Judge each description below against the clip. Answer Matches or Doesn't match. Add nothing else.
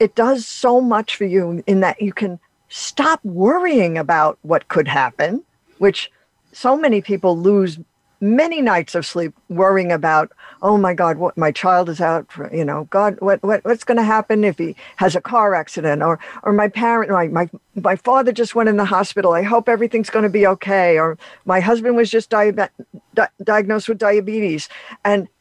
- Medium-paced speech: Matches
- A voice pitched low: Doesn't match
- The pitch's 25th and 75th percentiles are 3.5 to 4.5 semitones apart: Matches